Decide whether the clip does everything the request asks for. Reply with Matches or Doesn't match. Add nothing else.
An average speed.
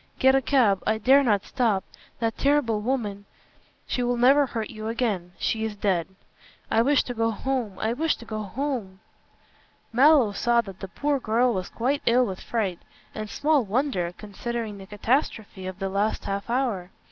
Matches